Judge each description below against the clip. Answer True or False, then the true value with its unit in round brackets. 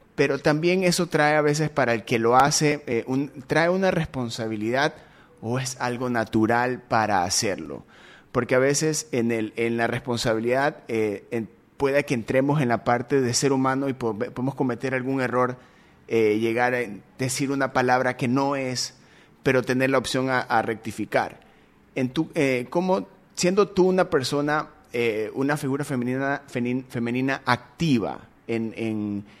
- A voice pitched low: True (130 Hz)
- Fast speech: False (160 wpm)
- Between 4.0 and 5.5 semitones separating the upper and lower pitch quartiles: False (3.2 semitones)